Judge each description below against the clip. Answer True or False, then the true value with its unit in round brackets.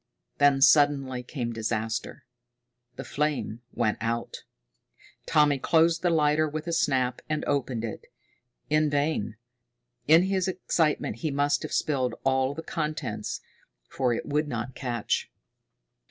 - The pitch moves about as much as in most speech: True (3.7 semitones)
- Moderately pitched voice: True (145 Hz)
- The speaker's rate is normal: False (130 wpm)